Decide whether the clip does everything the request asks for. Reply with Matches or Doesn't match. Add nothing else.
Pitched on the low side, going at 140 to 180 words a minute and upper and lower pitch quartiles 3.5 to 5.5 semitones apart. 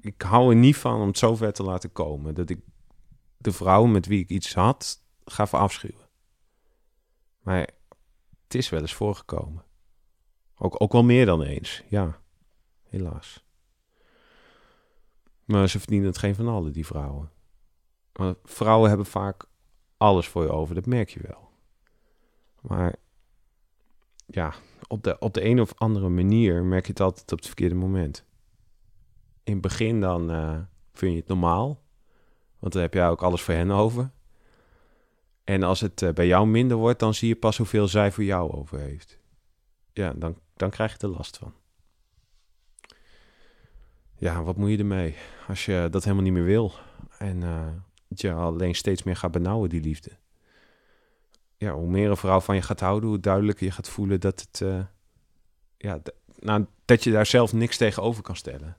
Matches